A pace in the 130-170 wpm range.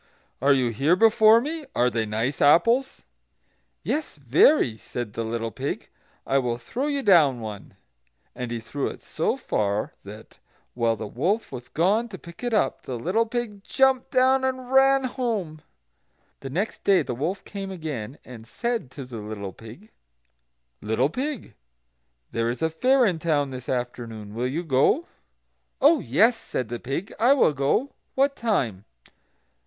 Yes: average, 165 wpm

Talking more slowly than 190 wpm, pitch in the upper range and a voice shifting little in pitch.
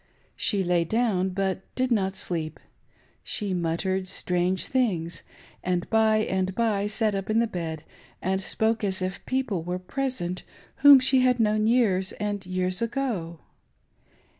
No: average, 145 wpm; high, 195 Hz; average, 3.6 semitones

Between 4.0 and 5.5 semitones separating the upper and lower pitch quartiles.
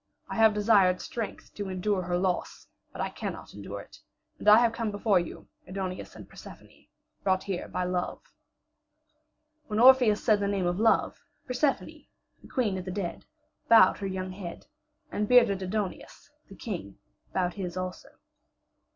No: average, 2.8 semitones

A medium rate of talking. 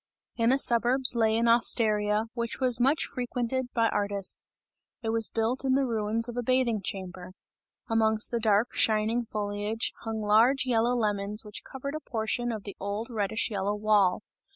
Yes: average, 170 wpm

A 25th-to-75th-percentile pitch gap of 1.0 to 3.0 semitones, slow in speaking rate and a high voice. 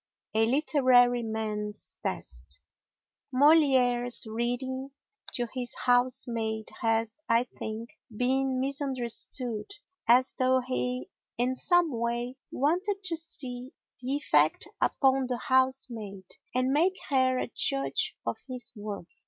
Yes: narrow, 2.5 semitones; slow, 110 wpm; very high, 250 Hz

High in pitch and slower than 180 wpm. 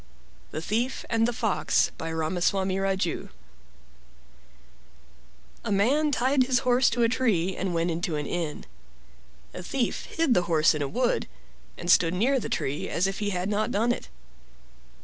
Yes: high, 195 Hz; average, 165 wpm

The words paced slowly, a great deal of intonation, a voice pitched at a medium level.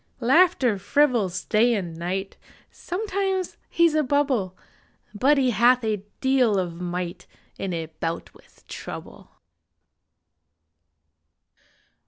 No: slow, 110 wpm; wide, 7.6 semitones; high, 230 Hz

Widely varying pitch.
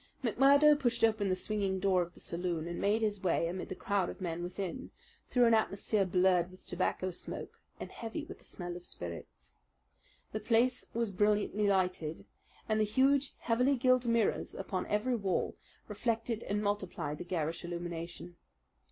No: average, 4.4 semitones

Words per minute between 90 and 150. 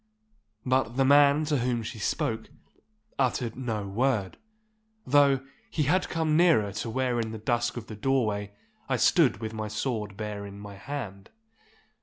No: average, 160 wpm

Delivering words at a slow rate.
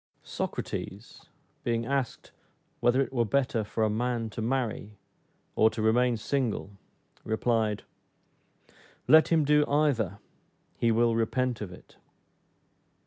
Yes: slow, 120 wpm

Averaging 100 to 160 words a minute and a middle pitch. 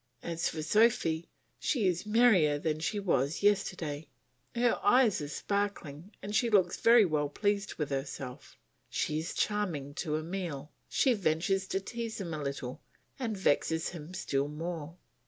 Yes: average, 155 wpm; medium, 175 Hz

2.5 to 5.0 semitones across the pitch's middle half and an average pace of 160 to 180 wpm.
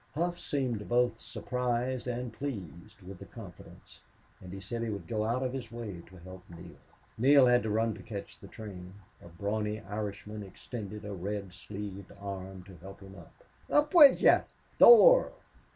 Yes: average, 4.1 semitones; average, 175 wpm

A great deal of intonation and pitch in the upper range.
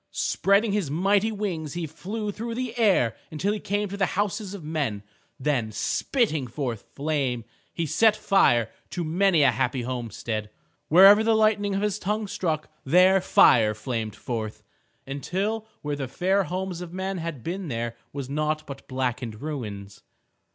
No: wide, 7.6 semitones; medium, 160 Hz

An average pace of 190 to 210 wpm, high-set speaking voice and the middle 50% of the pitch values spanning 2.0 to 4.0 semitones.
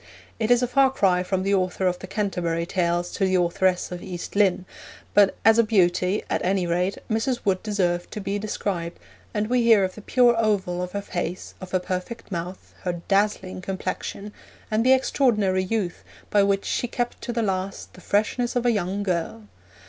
Yes: average, 195 wpm; high, 195 Hz; average, 3.0 semitones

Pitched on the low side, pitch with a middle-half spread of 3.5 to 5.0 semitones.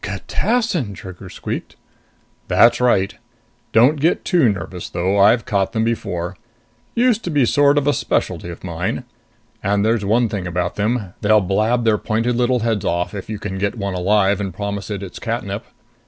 Yes: low, 105 Hz; average, 3.9 semitones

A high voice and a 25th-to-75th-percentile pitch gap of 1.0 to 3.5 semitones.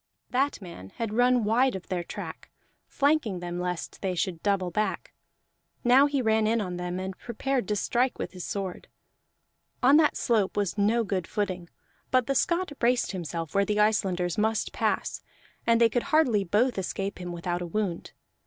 No: high, 210 Hz; average, 5.0 semitones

